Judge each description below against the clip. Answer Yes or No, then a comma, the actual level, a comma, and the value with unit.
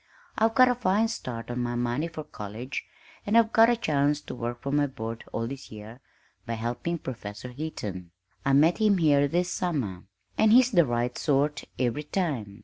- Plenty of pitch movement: Yes, wide, 6.7 semitones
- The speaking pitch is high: No, medium, 140 Hz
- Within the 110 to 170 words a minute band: No, average, 190 wpm